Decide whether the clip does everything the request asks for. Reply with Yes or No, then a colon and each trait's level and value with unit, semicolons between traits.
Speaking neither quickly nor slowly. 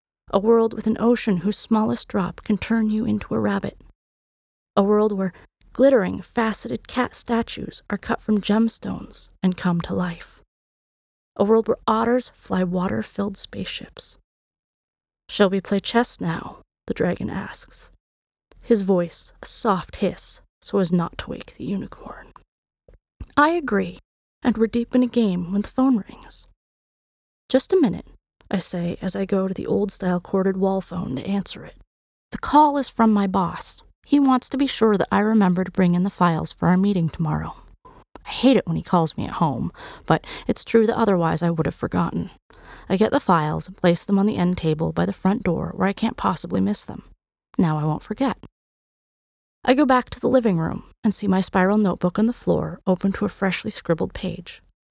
Yes: average, 190 wpm